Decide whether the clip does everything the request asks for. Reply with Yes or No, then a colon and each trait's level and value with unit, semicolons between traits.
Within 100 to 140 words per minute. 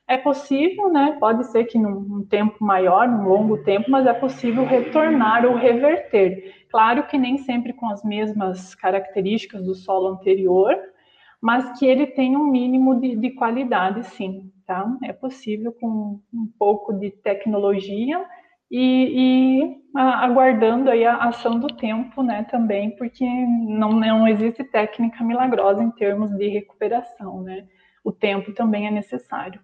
No: average, 150 wpm